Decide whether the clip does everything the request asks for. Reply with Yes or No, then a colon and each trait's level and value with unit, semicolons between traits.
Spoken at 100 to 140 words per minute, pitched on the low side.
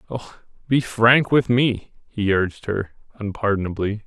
Yes: slow, 135 wpm; low, 110 Hz